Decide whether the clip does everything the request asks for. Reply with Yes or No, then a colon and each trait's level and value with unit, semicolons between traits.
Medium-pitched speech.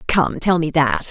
Yes: medium, 160 Hz